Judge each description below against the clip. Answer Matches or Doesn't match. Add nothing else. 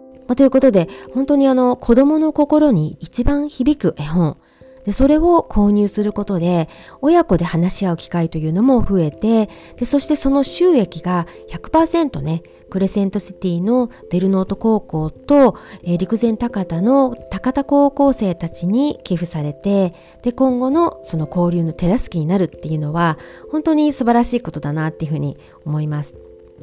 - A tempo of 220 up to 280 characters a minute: Doesn't match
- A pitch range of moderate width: Doesn't match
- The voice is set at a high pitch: Matches